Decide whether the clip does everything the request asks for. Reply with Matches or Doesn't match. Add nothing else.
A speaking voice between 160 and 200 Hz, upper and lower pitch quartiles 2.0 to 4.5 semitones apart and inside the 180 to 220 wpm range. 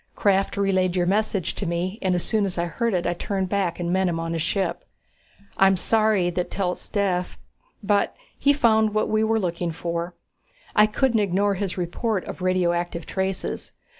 Matches